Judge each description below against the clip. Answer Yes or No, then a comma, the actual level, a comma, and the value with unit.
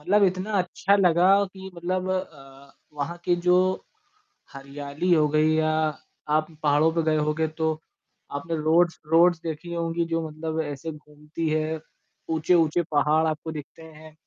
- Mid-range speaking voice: Yes, medium, 160 Hz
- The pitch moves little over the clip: Yes, narrow, 2.1 semitones